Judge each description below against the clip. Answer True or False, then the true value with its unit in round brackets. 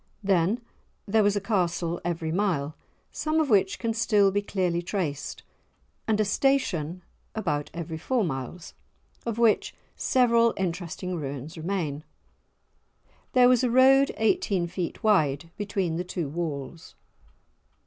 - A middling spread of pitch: True (5.0 semitones)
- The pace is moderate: False (130 wpm)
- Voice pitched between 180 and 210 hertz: True (185 Hz)